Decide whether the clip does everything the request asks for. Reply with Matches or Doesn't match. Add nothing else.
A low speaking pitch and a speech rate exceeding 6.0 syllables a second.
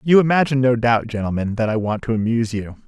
Matches